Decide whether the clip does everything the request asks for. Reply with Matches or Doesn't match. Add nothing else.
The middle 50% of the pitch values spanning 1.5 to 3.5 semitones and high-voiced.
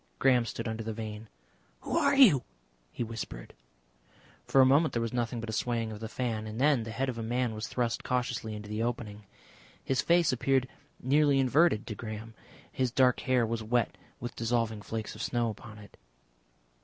Doesn't match